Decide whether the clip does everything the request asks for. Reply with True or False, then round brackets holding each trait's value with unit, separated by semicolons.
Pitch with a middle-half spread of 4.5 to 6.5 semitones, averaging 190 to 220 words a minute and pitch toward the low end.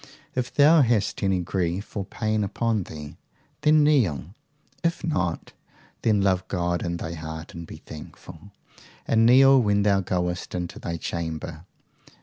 False (5.1 semitones; 145 wpm; 95 Hz)